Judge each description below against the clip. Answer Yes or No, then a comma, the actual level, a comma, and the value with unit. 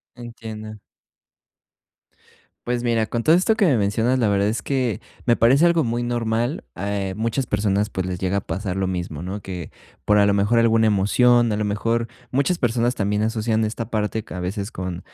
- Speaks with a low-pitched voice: Yes, low, 110 Hz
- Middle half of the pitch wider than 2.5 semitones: Yes, average, 2.9 semitones